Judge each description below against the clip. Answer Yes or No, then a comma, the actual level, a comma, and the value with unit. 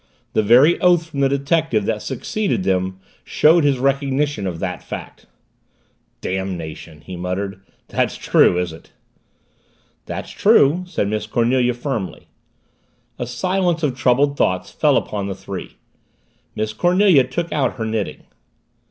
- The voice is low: Yes, low, 125 Hz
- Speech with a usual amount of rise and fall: No, wide, 7.0 semitones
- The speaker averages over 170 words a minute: No, slow, 135 wpm